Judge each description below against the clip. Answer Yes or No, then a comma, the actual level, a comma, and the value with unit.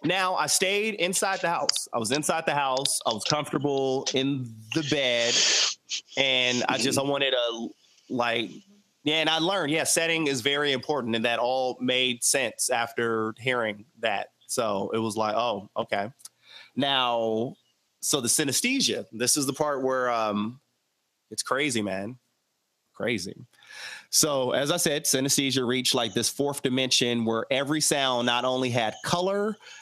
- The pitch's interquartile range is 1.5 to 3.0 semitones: No, average, 4.0 semitones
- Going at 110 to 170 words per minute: Yes, average, 155 wpm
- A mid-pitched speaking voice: No, low, 130 Hz